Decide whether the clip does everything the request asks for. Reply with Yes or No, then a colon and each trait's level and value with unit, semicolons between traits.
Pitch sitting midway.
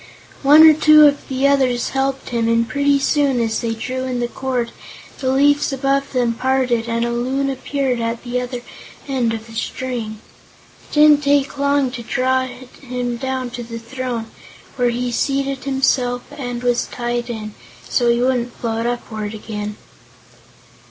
No: very high, 250 Hz